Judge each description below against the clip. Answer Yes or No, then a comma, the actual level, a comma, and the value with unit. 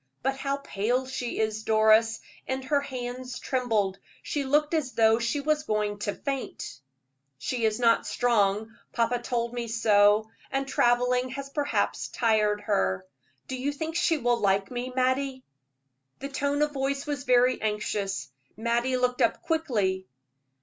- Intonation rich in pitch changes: No, average, 3.8 semitones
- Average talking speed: Yes, average, 150 wpm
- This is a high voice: Yes, high, 245 Hz